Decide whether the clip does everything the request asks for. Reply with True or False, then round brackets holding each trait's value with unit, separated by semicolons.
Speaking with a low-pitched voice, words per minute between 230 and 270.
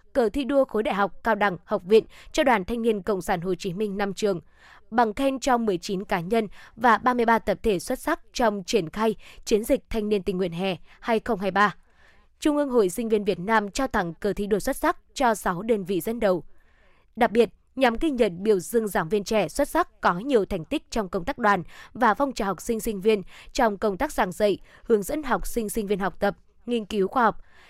False (220 Hz; 235 wpm)